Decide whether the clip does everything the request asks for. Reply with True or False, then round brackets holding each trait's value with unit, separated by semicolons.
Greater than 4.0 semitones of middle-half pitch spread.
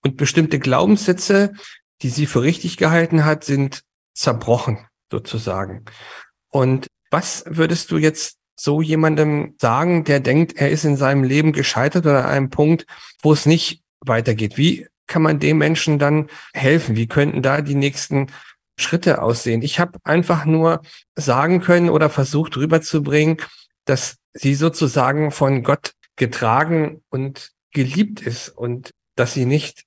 False (3.2 semitones)